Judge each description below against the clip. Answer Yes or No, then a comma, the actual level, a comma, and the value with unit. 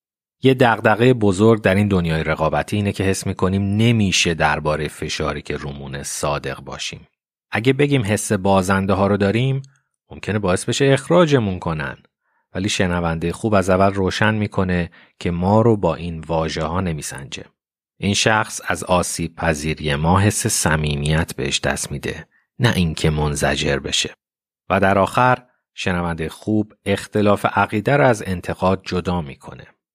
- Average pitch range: Yes, average, 4.6 semitones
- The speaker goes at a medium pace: Yes, average, 145 wpm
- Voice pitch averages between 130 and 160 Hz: No, very low, 95 Hz